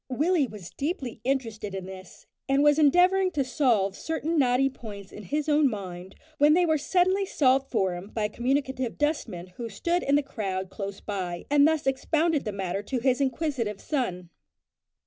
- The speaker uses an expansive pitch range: Yes, wide, 6.7 semitones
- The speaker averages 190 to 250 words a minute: No, average, 180 wpm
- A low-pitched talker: No, very high, 260 Hz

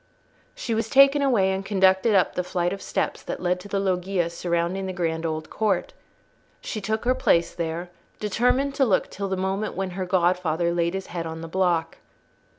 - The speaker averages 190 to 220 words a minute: Yes, average, 195 wpm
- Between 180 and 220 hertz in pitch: Yes, medium, 185 Hz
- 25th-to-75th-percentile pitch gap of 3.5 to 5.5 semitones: No, average, 2.8 semitones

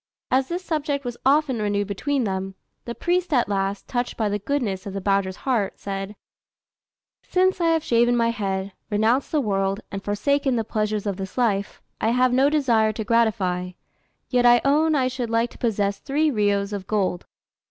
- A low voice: No, high, 225 Hz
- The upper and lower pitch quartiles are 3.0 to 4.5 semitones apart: No, average, 5.0 semitones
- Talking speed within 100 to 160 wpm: No, average, 185 wpm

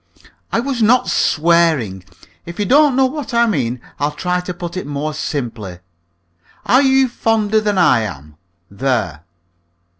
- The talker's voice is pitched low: No, medium, 170 Hz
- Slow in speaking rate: No, average, 150 wpm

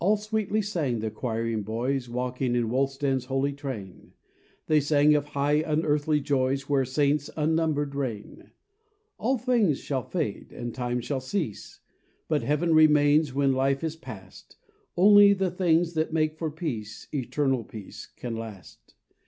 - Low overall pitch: No, medium, 145 Hz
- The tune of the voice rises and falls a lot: No, average, 3.8 semitones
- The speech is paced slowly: No, average, 150 wpm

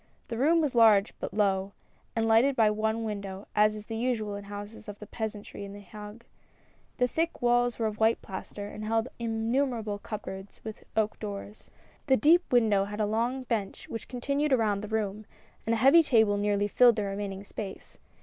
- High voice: Yes, high, 220 Hz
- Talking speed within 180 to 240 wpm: Yes, average, 190 wpm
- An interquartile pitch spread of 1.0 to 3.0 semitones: Yes, narrow, 2.6 semitones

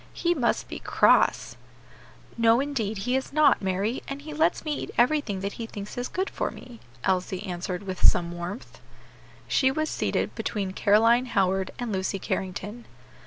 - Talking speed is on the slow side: No, average, 165 wpm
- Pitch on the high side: Yes, high, 225 Hz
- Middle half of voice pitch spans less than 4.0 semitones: No, wide, 5.6 semitones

